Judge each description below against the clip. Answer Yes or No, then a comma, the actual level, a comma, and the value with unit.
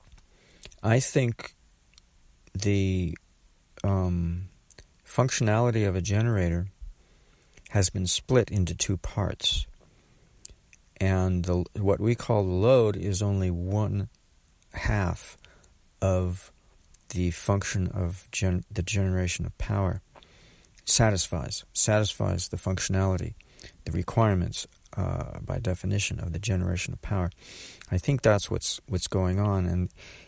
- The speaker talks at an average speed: No, slow, 110 wpm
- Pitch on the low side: Yes, very low, 95 Hz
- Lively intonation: No, average, 2.8 semitones